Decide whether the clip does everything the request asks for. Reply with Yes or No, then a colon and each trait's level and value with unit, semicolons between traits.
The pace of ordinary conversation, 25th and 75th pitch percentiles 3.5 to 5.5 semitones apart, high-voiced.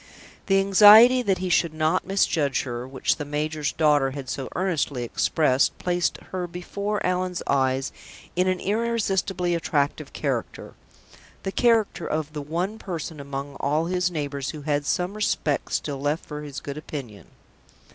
No: average, 155 wpm; average, 4.6 semitones; medium, 155 Hz